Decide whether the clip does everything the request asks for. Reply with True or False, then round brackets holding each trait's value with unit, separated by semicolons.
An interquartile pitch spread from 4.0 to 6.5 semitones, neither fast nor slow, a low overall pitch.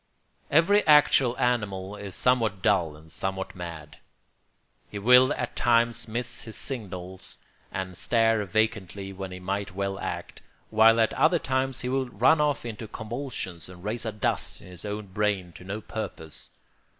True (4.3 semitones; 160 wpm; 105 Hz)